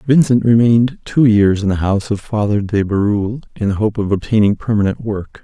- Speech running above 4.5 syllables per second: Yes, 5.6 syllables/s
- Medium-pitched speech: No, low, 105 Hz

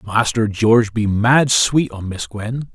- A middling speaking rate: Yes, average, 175 wpm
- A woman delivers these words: No, male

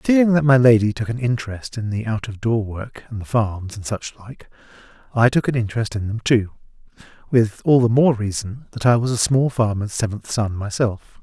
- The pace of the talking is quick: Yes, fast, 210 wpm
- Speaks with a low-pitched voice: Yes, low, 115 Hz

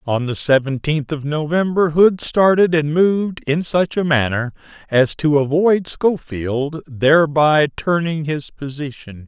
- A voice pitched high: No, medium, 155 Hz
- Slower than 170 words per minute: Yes, slow, 135 wpm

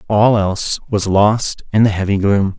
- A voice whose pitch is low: Yes, low, 100 Hz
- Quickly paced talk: No, average, 185 wpm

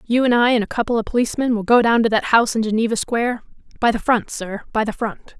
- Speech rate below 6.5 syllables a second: No, 6.6 syllables/s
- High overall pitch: Yes, high, 230 Hz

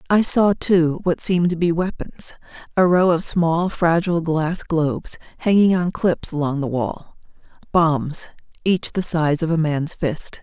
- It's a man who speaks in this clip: No, female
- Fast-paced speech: No, average, 160 wpm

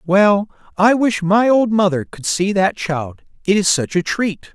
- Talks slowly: No, average, 200 wpm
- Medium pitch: No, high, 195 Hz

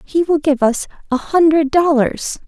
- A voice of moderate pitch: No, very high, 295 Hz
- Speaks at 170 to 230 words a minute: No, average, 145 wpm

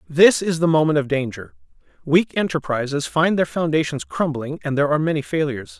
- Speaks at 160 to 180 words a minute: Yes, average, 175 wpm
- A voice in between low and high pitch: Yes, medium, 145 Hz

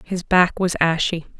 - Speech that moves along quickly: No, average, 170 wpm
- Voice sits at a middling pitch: Yes, medium, 175 Hz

